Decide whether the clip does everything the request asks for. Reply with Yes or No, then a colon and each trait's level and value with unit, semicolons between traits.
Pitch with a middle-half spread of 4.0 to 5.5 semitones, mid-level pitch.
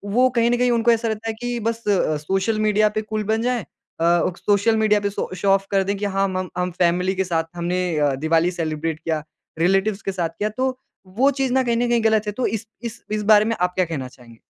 No: average, 4.3 semitones; high, 205 Hz